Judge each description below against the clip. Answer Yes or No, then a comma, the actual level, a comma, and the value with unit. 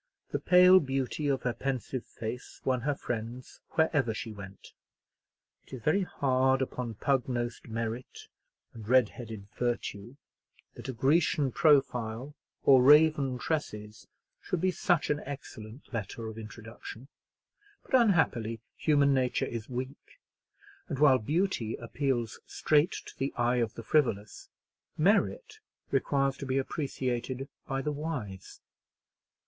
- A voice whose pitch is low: Yes, low, 130 Hz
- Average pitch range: Yes, average, 4.1 semitones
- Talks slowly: Yes, slow, 130 wpm